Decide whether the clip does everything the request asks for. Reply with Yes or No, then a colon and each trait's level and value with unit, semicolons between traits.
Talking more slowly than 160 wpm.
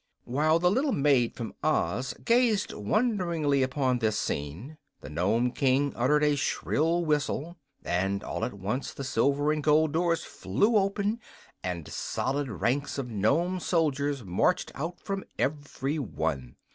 Yes: average, 145 wpm